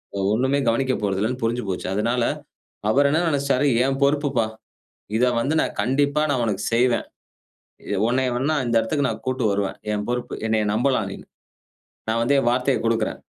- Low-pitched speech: Yes, low, 125 Hz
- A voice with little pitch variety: No, average, 3.6 semitones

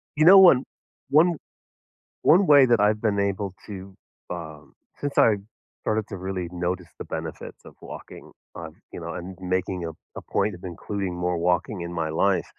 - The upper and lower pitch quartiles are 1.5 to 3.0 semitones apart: No, average, 3.6 semitones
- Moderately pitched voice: No, very low, 95 Hz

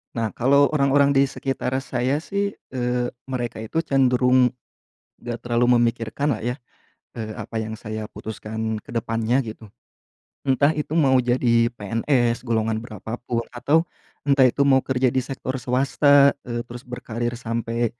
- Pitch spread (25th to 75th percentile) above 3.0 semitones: No, average, 2.7 semitones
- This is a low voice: Yes, low, 125 Hz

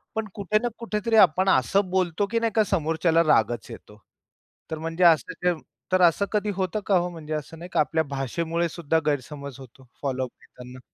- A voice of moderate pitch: Yes, medium, 165 Hz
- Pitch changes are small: No, average, 4.6 semitones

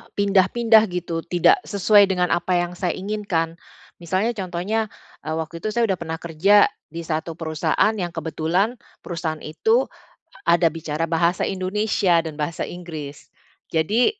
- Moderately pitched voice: Yes, medium, 175 Hz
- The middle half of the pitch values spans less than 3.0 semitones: No, average, 3.7 semitones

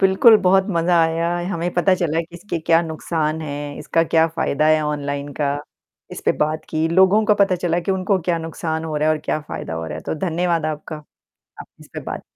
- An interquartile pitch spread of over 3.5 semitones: No, narrow, 2.5 semitones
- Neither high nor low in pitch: Yes, medium, 165 Hz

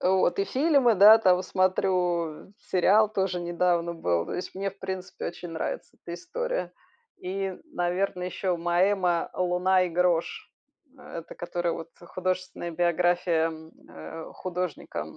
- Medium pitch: Yes, medium, 180 Hz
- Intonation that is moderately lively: No, narrow, 1.7 semitones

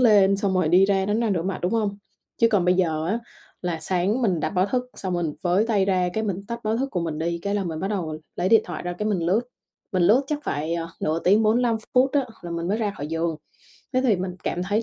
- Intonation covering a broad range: No, average, 3.8 semitones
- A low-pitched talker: No, high, 190 Hz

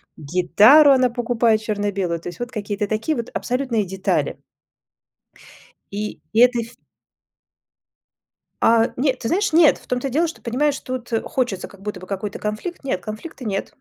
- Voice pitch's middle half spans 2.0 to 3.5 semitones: No, average, 4.1 semitones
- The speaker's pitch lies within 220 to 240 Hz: Yes, high, 230 Hz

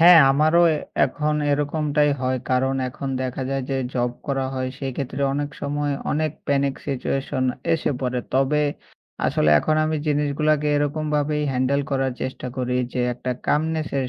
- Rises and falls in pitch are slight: Yes, narrow, 2.3 semitones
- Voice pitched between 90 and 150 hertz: Yes, medium, 140 Hz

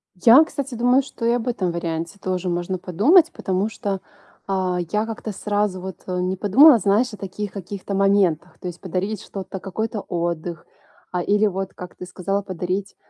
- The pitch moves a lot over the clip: No, average, 2.8 semitones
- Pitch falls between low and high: No, high, 195 Hz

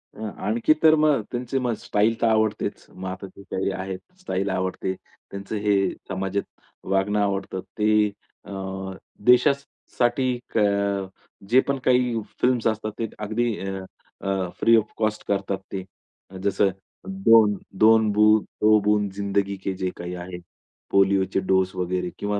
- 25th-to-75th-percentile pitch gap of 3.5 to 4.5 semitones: No, average, 2.8 semitones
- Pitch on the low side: Yes, low, 105 Hz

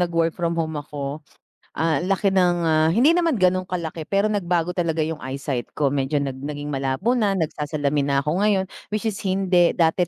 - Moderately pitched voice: Yes, medium, 165 Hz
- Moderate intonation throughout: Yes, average, 4.3 semitones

